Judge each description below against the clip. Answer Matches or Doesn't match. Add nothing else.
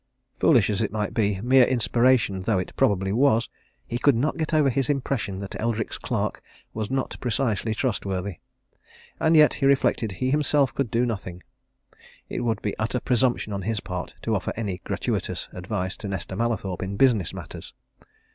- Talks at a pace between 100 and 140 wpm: Doesn't match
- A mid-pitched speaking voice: Doesn't match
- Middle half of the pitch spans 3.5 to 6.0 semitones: Matches